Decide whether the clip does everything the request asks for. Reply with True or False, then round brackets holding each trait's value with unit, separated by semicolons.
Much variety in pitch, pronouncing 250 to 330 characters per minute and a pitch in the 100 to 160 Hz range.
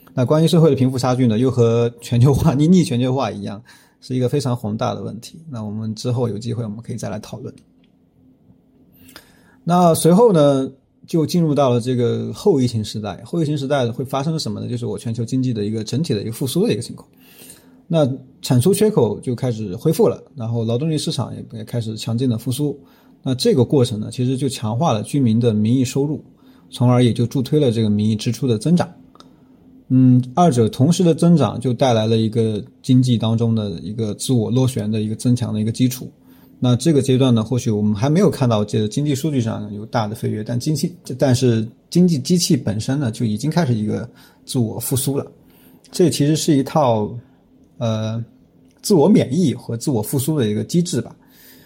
False (4.2 semitones; 310 characters per minute; 125 Hz)